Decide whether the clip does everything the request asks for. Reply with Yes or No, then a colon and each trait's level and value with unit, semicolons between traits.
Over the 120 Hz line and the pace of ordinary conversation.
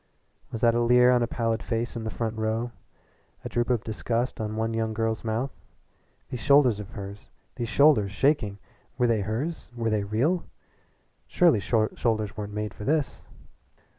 No: low, 115 Hz; average, 170 wpm